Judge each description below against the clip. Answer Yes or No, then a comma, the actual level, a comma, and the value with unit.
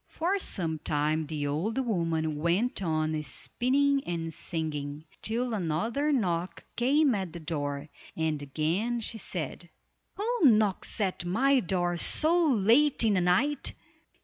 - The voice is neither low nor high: Yes, medium, 180 Hz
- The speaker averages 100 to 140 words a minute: Yes, slow, 135 wpm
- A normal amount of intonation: No, wide, 7.6 semitones